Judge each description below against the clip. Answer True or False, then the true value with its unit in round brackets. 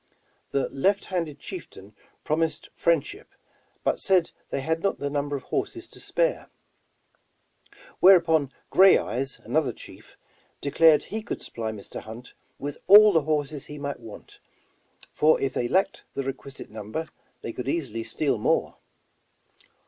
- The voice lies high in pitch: False (145 Hz)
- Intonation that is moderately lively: True (3.9 semitones)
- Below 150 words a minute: True (140 wpm)